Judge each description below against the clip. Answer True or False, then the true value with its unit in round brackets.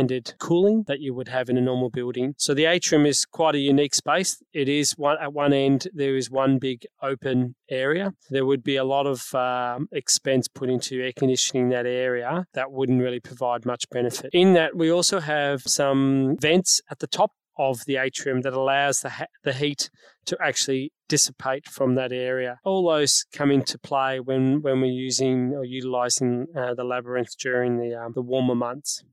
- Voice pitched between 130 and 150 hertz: True (135 Hz)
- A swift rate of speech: False (195 wpm)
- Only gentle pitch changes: True (2.3 semitones)